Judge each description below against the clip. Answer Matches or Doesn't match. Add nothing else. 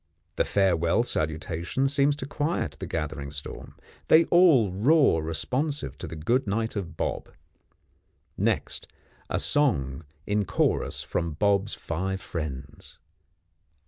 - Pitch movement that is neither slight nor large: Doesn't match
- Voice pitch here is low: Matches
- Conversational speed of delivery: Doesn't match